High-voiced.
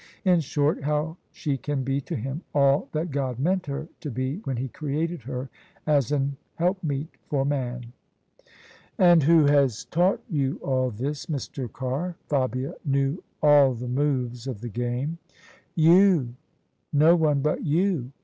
No: medium, 140 Hz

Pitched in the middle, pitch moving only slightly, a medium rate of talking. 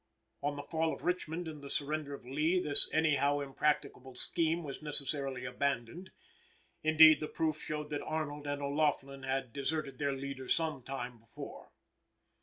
Yes: medium, 145 Hz; narrow, 2.3 semitones; average, 160 wpm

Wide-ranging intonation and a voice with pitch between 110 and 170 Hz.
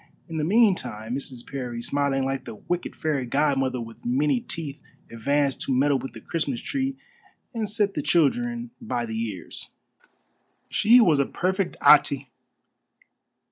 Yes: wide, 6.2 semitones; medium, 140 Hz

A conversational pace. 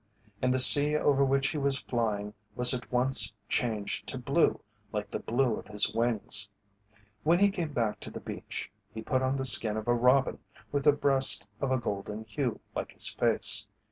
Yes: average, 195 wpm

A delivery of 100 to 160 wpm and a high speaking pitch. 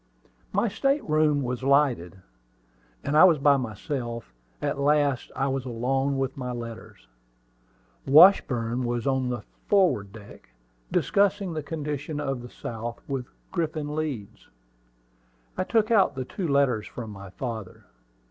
No: average, 140 wpm; low, 135 Hz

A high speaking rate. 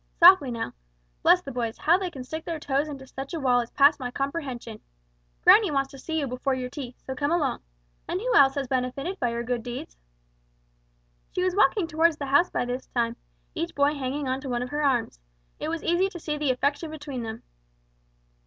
Yes: fast, 220 wpm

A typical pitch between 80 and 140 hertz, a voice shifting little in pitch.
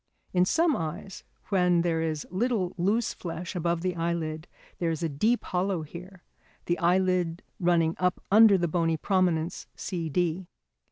No: medium, 175 Hz; narrow, 2.1 semitones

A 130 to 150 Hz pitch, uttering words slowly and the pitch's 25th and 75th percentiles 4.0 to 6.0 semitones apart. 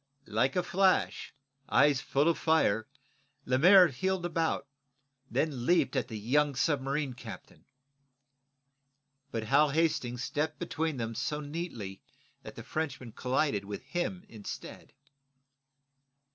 Yes: medium, 140 Hz; slow, 120 wpm; average, 4.5 semitones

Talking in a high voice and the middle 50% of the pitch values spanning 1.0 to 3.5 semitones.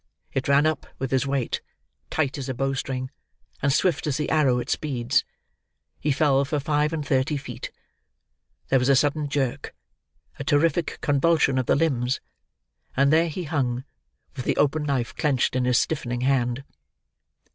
No: medium, 140 Hz; narrow, 2.4 semitones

